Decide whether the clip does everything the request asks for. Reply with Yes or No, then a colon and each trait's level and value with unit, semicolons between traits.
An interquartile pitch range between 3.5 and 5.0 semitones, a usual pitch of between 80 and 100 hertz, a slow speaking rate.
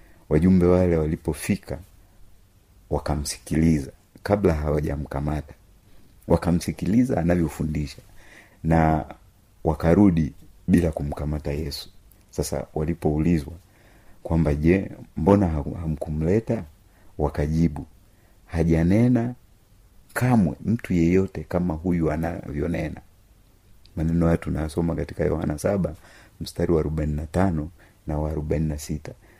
Yes: average, 4.0 semitones; very low, 85 Hz; slow, 90 wpm